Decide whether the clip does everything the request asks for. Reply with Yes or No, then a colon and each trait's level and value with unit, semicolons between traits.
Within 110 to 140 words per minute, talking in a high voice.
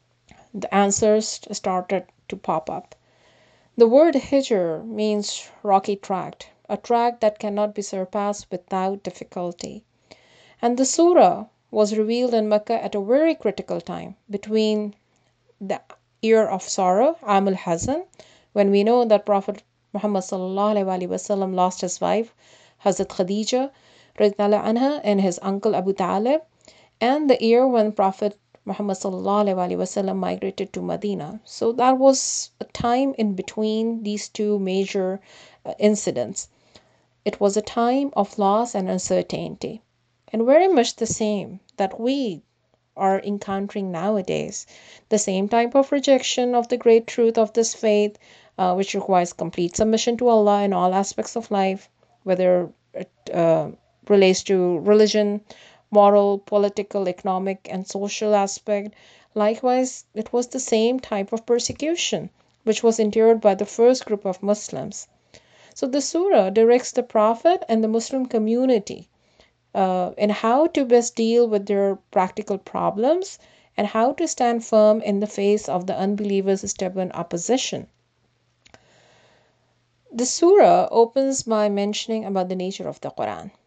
Yes: slow, 135 wpm; high, 210 Hz